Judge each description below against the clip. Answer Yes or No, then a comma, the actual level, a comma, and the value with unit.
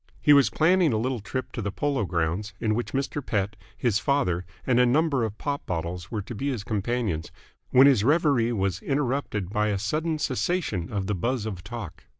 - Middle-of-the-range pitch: No, low, 115 Hz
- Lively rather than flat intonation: Yes, wide, 5.8 semitones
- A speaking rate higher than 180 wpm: Yes, average, 200 wpm